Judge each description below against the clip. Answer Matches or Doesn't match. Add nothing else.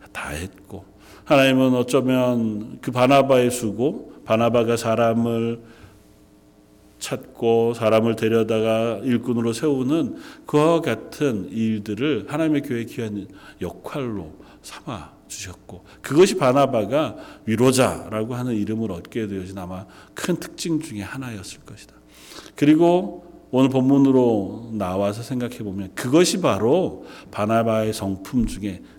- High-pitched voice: Doesn't match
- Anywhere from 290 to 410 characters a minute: Doesn't match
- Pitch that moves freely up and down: Doesn't match